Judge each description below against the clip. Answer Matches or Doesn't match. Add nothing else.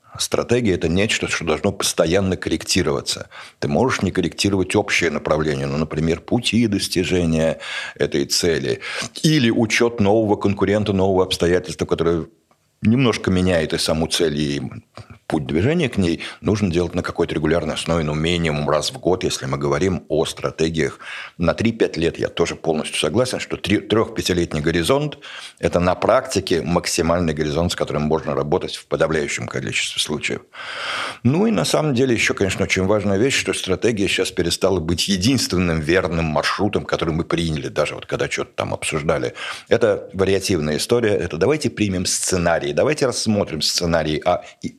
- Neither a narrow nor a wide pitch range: Matches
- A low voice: Matches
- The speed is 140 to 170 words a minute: Matches